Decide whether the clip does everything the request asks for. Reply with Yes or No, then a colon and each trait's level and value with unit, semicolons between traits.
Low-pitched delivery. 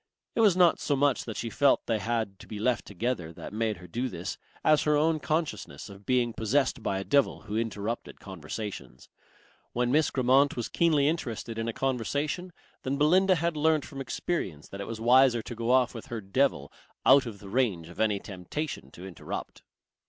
Yes: low, 120 Hz